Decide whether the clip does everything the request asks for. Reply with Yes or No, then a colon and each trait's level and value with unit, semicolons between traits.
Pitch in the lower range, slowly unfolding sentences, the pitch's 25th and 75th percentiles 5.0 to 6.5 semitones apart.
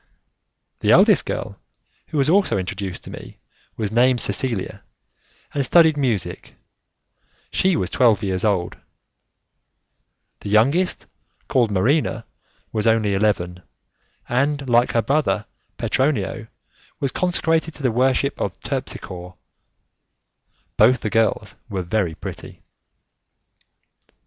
Yes: low, 115 Hz; slow, 110 wpm; wide, 5.4 semitones